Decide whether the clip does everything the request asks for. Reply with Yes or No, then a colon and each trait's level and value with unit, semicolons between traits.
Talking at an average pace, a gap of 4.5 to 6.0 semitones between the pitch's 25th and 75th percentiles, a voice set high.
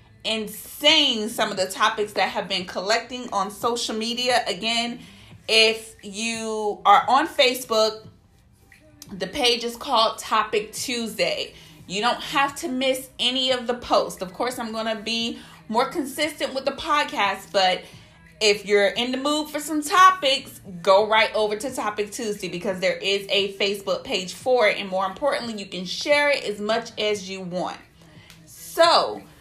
Yes: average, 165 wpm; average, 4.8 semitones; high, 225 Hz